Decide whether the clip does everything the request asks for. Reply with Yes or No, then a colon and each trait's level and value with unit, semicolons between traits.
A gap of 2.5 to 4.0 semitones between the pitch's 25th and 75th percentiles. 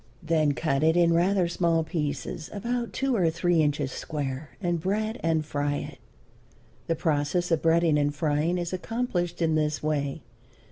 Yes: average, 2.9 semitones